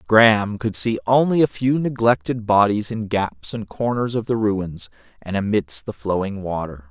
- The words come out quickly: No, average, 175 wpm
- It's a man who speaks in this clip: Yes, male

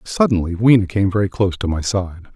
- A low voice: Yes, very low, 95 Hz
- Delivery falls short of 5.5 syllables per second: No, 6.0 syllables/s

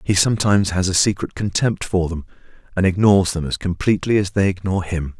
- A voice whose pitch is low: Yes, very low, 95 Hz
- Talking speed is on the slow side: No, average, 195 wpm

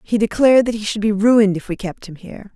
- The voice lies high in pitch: Yes, high, 210 Hz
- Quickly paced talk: Yes, fast, 280 wpm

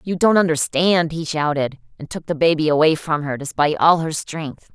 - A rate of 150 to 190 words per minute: No, average, 200 wpm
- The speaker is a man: No, female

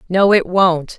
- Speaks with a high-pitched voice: No, medium, 180 Hz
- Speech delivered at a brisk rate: No, average, 185 wpm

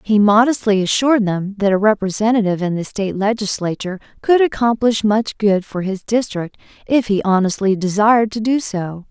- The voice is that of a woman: Yes, female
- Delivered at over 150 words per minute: Yes, average, 165 wpm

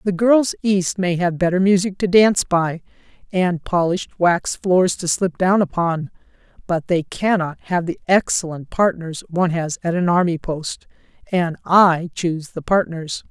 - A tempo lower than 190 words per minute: Yes, average, 160 wpm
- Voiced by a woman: Yes, female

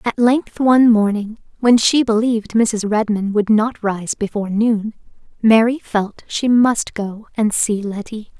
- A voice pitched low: No, high, 220 Hz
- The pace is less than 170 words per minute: Yes, average, 155 wpm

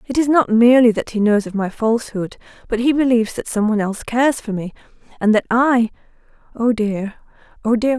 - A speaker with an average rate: Yes, average, 195 wpm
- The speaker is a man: No, female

